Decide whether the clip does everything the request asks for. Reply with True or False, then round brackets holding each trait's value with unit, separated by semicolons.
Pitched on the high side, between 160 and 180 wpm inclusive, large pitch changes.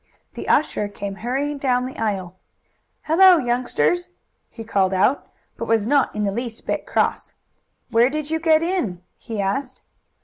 True (245 Hz; 165 wpm; 6.1 semitones)